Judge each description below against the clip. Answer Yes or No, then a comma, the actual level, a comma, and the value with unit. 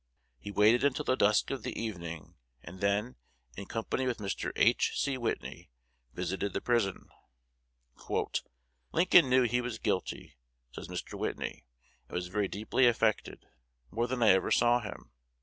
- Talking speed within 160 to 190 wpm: No, average, 150 wpm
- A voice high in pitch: No, low, 110 Hz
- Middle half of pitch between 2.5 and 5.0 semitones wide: Yes, average, 3.8 semitones